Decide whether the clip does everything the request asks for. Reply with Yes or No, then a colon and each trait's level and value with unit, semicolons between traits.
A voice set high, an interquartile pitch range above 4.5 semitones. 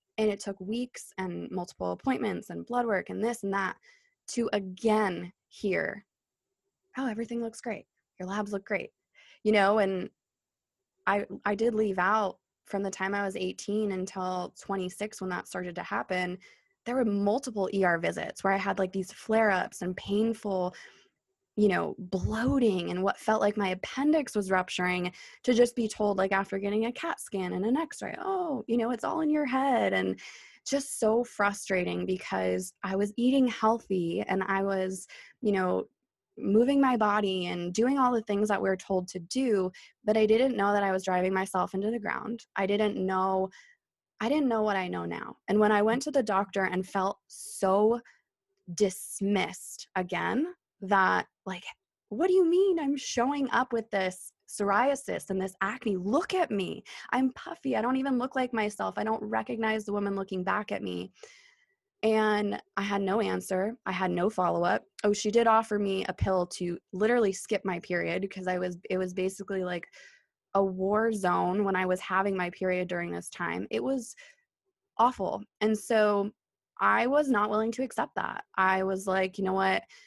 No: high, 205 Hz; average, 3.9 semitones